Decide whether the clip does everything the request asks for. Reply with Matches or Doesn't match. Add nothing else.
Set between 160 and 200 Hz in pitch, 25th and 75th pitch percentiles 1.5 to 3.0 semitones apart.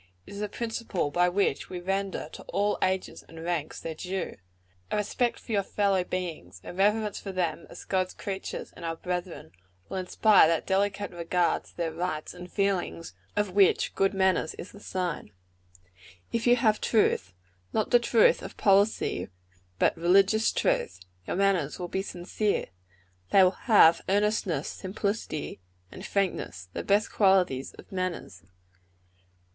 Matches